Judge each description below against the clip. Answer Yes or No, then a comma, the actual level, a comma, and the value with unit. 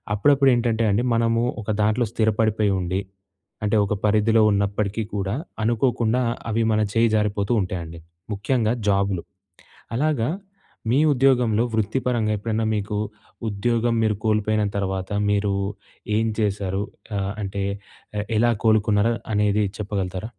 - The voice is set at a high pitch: No, low, 105 Hz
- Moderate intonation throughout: No, narrow, 2.3 semitones